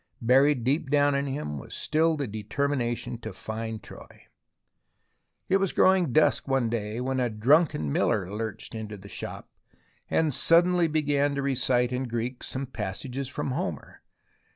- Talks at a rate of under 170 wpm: Yes, average, 155 wpm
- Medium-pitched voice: No, low, 130 Hz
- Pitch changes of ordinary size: Yes, average, 4.5 semitones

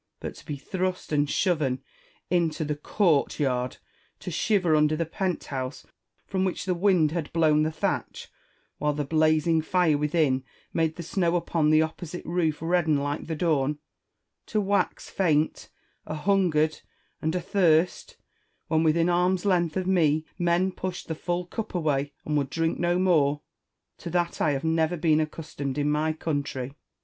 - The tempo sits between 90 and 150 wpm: No, average, 165 wpm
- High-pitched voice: No, medium, 160 Hz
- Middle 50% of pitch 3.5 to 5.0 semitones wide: No, average, 2.8 semitones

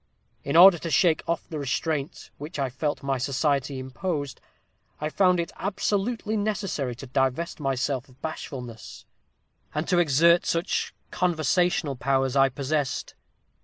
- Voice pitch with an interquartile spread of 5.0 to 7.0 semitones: No, average, 4.4 semitones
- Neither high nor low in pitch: Yes, medium, 150 Hz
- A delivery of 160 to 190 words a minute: No, average, 140 wpm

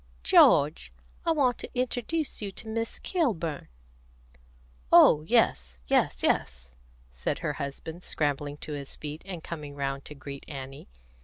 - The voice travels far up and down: Yes, wide, 7.8 semitones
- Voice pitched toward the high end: No, medium, 150 Hz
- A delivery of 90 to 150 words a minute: Yes, average, 140 wpm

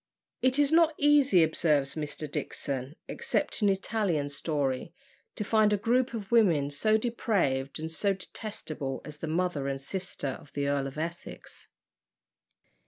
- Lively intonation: Yes, wide, 7.3 semitones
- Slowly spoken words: No, average, 150 wpm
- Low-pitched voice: No, medium, 170 Hz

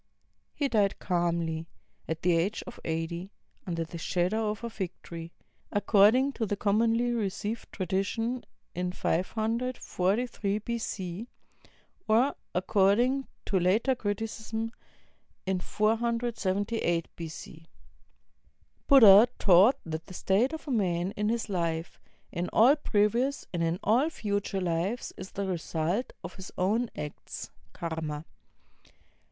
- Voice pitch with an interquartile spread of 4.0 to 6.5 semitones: Yes, average, 4.7 semitones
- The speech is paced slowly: Yes, slow, 125 wpm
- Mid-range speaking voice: No, high, 200 Hz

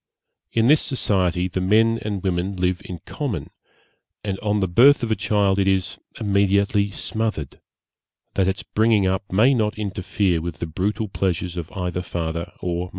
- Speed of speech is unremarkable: Yes, average, 170 wpm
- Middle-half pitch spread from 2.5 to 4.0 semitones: Yes, average, 2.9 semitones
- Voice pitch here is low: Yes, very low, 95 Hz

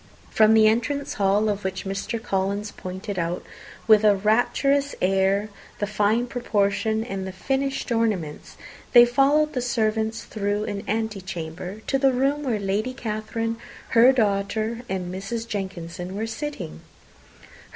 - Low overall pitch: No, high, 215 Hz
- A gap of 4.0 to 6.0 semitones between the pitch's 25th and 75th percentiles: No, average, 3.3 semitones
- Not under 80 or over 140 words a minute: Yes, slow, 135 wpm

